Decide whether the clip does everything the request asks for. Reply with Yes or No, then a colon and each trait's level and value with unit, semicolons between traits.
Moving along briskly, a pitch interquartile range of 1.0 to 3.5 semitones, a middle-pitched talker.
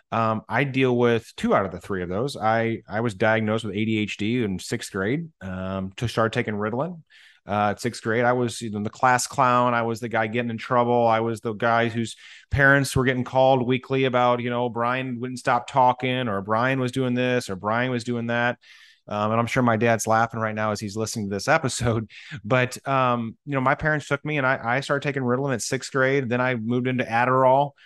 No: fast, 230 wpm; narrow, 2.6 semitones; low, 120 Hz